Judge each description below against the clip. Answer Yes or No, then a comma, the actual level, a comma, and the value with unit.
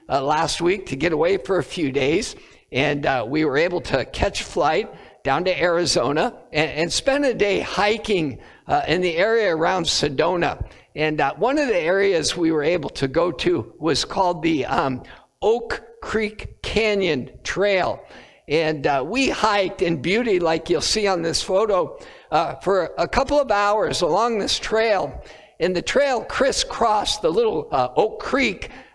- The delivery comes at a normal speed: Yes, average, 170 wpm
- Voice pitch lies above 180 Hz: Yes, high, 190 Hz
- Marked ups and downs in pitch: Yes, wide, 6.2 semitones